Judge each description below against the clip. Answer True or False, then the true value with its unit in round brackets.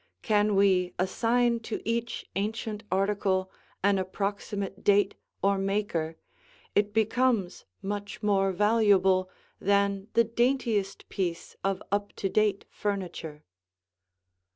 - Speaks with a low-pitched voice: False (200 Hz)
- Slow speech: True (105 wpm)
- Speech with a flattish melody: True (1.8 semitones)